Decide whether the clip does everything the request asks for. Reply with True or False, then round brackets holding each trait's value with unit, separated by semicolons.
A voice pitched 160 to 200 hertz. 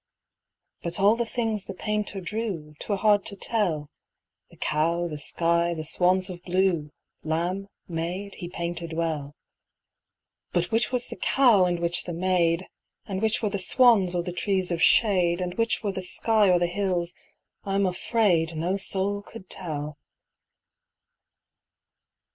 True (185 Hz)